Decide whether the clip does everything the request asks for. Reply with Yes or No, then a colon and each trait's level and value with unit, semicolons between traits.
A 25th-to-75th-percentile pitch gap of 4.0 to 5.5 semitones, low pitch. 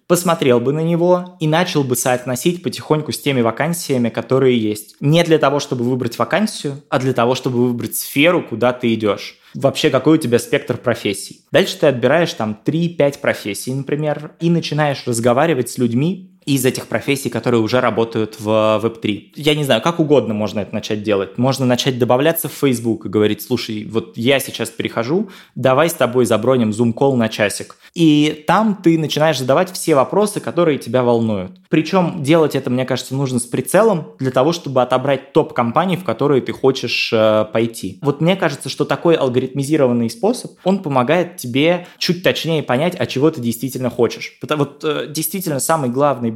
Yes: average, 4.9 semitones; low, 130 Hz